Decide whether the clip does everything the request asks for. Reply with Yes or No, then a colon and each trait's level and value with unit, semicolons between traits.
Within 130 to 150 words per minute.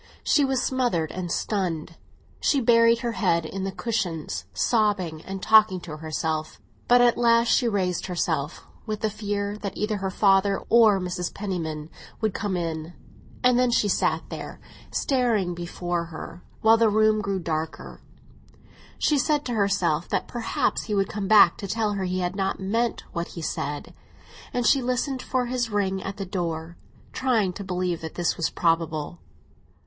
No: average, 170 wpm